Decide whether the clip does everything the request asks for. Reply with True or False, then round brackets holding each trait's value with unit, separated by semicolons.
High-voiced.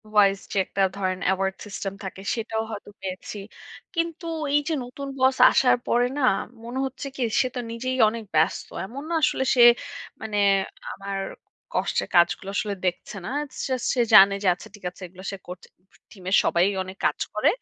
True (205 Hz)